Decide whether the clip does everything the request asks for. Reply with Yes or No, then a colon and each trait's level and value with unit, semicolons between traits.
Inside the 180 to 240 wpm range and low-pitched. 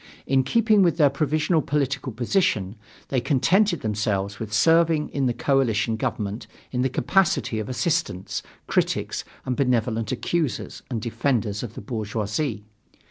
No: slow, 135 wpm; low, 125 Hz